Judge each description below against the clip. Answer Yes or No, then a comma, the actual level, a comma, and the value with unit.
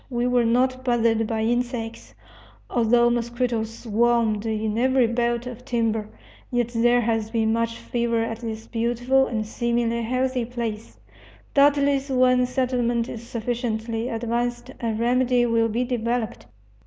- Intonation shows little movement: Yes, narrow, 1.5 semitones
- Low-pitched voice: No, high, 235 Hz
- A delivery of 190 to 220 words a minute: No, slow, 135 wpm